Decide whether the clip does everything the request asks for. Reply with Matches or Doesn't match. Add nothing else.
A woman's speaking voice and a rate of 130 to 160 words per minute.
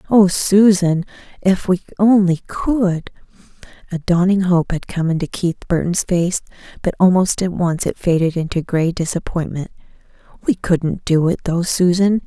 Matches